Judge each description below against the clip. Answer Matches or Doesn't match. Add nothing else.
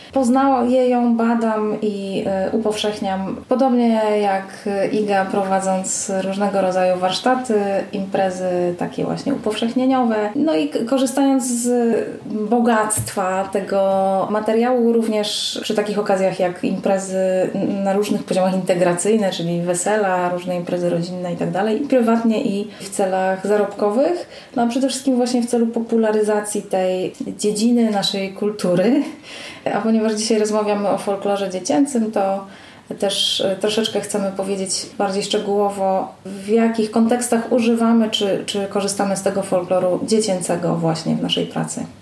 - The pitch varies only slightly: Doesn't match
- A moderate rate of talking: Matches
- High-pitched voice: Matches